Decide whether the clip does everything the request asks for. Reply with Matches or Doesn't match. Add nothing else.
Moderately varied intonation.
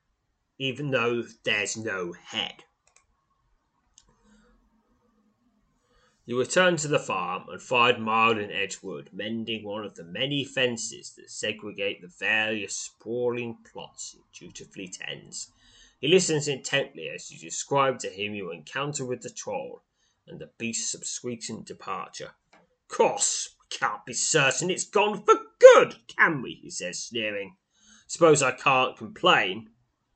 Doesn't match